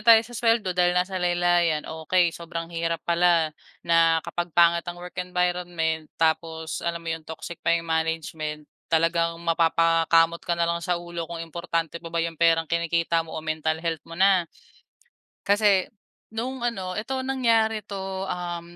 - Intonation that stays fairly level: Yes, narrow, 1.5 semitones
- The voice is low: No, medium, 170 Hz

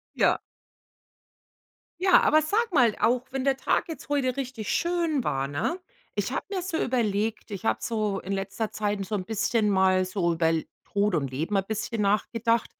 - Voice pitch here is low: No, high, 215 Hz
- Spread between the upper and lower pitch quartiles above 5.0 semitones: Yes, wide, 5.4 semitones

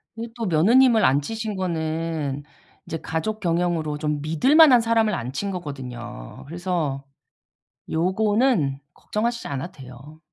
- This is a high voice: No, medium, 165 Hz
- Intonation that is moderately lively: No, wide, 6.9 semitones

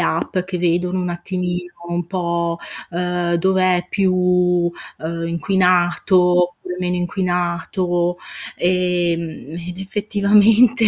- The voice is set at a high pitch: No, medium, 180 Hz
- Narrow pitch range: Yes, narrow, 1.2 semitones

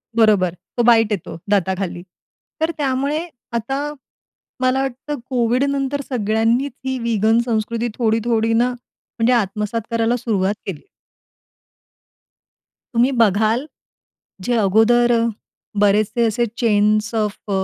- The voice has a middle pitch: No, high, 230 Hz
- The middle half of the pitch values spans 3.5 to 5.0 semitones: No, average, 2.8 semitones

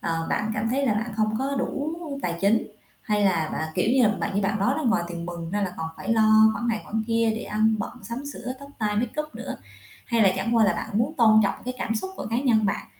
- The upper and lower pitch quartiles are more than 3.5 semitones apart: No, average, 2.9 semitones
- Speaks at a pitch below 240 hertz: Yes, high, 220 Hz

